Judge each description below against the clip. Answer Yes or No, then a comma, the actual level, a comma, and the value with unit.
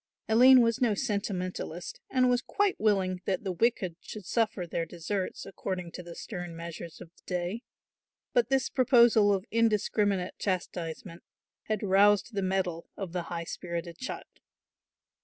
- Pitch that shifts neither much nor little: Yes, average, 4.0 semitones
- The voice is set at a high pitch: Yes, high, 195 Hz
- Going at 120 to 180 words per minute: Yes, average, 150 wpm